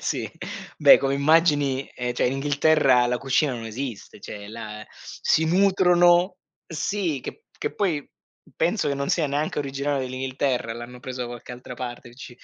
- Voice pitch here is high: No, low, 135 Hz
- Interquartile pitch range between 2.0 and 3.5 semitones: No, average, 4.2 semitones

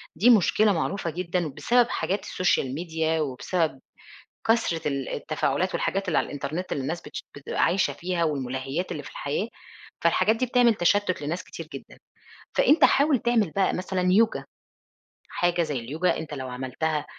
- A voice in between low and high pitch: Yes, medium, 170 Hz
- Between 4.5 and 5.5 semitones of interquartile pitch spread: Yes, average, 5.1 semitones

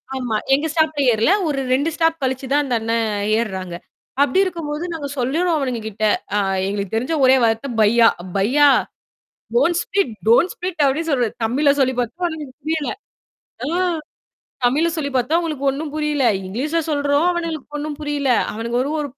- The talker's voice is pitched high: Yes, very high, 285 Hz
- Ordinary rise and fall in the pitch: Yes, average, 4.5 semitones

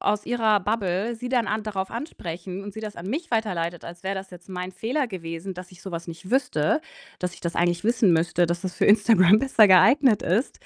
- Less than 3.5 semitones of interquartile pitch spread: No, average, 4.2 semitones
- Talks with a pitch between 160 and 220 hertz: Yes, high, 190 Hz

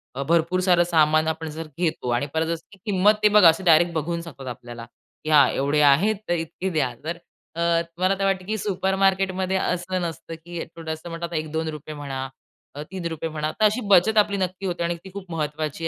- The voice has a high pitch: No, medium, 170 Hz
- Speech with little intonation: No, average, 3.0 semitones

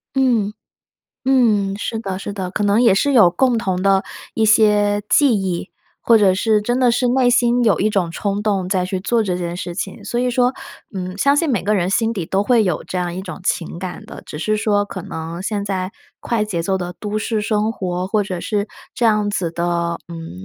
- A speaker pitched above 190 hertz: Yes, high, 205 Hz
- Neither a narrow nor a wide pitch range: Yes, average, 3.4 semitones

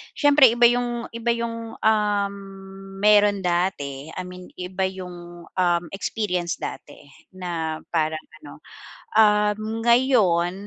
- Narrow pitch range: No, average, 4.5 semitones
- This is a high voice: Yes, high, 195 Hz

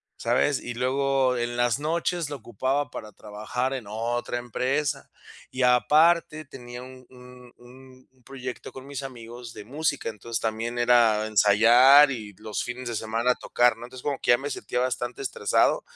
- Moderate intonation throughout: No, narrow, 2.3 semitones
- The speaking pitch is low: Yes, low, 125 Hz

